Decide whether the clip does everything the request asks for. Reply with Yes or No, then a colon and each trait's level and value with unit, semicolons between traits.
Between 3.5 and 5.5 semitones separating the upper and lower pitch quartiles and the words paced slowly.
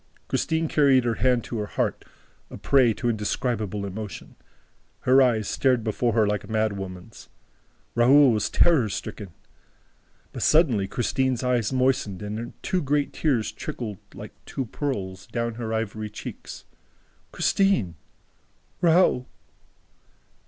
Yes: average, 3.8 semitones; slow, 130 wpm